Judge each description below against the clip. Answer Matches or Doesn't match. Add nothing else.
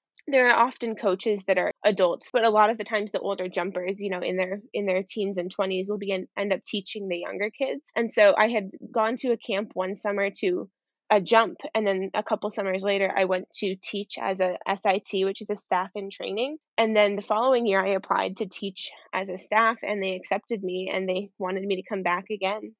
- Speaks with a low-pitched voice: Doesn't match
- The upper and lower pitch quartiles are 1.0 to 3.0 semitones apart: Matches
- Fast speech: Matches